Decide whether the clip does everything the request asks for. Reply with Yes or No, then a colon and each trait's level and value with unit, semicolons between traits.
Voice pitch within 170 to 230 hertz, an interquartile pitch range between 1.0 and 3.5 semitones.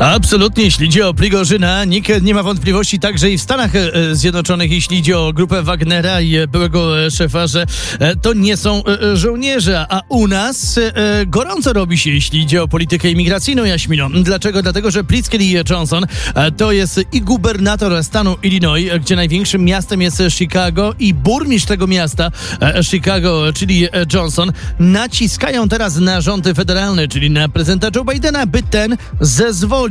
Yes: medium, 185 Hz; average, 3.2 semitones